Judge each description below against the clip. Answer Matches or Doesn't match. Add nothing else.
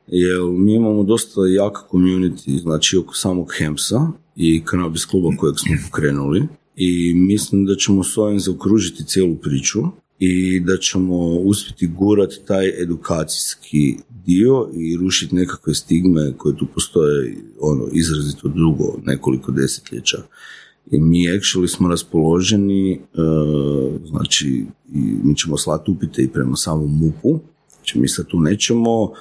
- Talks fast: Doesn't match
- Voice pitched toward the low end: Matches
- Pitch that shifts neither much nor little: Matches